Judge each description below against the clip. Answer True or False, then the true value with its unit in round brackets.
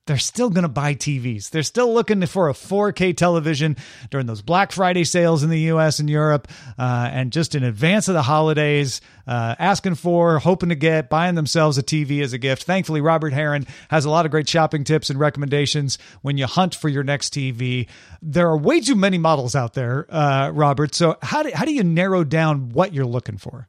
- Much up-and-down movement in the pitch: False (3.6 semitones)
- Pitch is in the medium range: True (155 Hz)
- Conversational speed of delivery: False (215 wpm)